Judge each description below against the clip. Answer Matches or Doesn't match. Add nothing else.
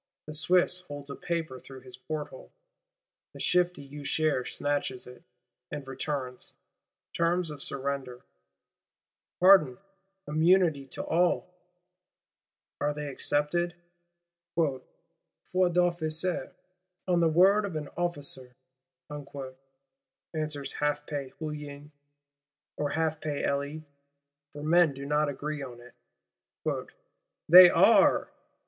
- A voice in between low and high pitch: Matches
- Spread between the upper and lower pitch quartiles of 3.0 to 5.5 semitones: Matches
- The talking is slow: Matches